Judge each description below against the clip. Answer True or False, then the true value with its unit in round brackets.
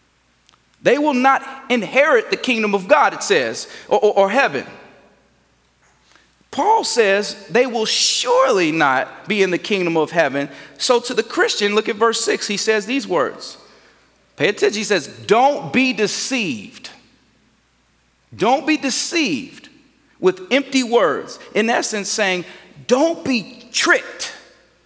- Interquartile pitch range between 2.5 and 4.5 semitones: False (5.3 semitones)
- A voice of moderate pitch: False (245 Hz)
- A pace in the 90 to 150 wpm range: True (140 wpm)